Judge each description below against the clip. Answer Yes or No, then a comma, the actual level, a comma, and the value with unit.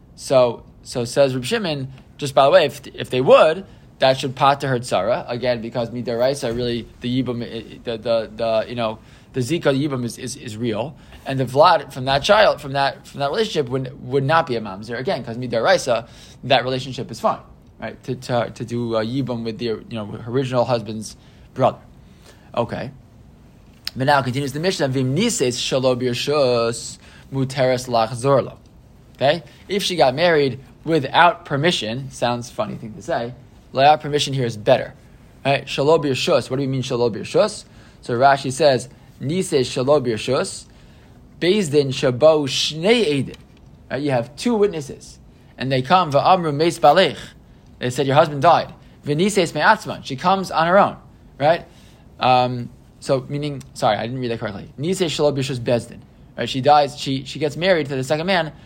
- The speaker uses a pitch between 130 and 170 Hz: Yes, low, 135 Hz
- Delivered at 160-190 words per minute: Yes, average, 170 wpm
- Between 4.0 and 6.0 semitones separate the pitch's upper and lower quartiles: No, average, 3.5 semitones